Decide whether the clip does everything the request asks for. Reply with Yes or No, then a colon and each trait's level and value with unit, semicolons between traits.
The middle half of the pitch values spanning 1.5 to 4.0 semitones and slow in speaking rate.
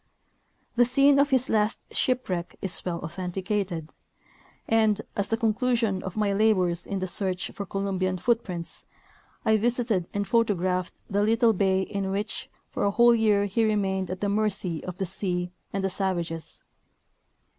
No: average, 3.0 semitones; average, 160 wpm